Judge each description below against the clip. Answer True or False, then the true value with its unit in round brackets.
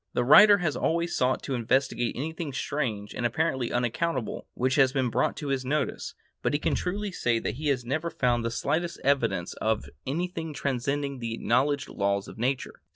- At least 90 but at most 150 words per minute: False (180 wpm)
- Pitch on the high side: False (135 Hz)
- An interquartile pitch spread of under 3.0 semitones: False (4.2 semitones)